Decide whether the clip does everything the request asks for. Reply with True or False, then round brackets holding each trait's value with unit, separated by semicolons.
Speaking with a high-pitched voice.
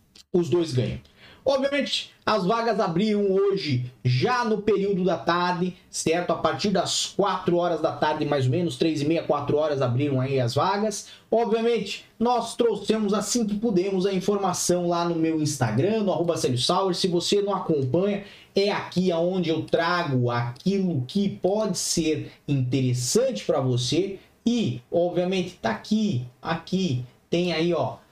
False (175 Hz)